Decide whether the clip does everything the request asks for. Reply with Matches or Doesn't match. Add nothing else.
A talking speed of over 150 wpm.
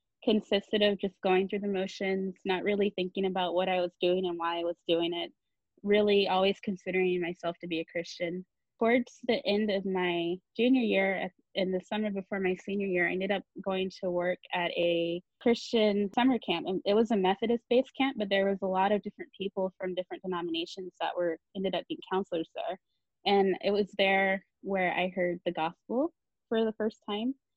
Matches